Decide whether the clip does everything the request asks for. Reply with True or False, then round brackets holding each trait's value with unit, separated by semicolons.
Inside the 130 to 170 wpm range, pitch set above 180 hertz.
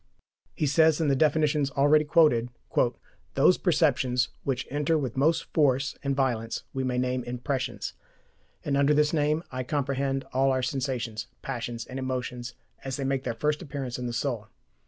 False (165 wpm; 135 Hz)